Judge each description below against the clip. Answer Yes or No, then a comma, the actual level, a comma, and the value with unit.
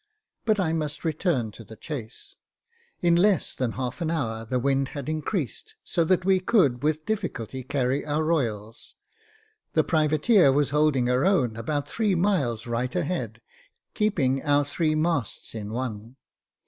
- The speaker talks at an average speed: Yes, average, 155 wpm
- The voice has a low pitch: No, medium, 145 Hz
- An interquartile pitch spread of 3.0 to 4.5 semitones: No, average, 5.3 semitones